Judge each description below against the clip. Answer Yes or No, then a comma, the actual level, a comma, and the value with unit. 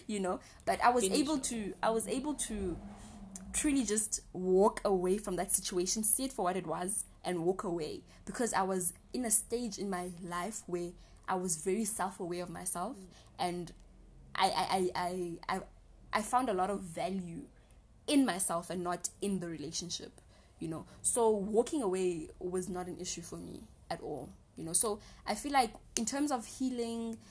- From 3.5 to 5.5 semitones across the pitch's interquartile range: Yes, average, 3.8 semitones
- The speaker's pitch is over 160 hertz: Yes, high, 190 Hz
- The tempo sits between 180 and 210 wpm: Yes, average, 185 wpm